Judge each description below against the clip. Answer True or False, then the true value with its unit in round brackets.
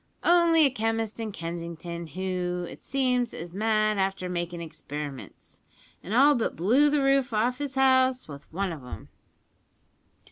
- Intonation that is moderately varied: False (7.0 semitones)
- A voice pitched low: False (215 Hz)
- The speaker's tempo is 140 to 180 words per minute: True (150 wpm)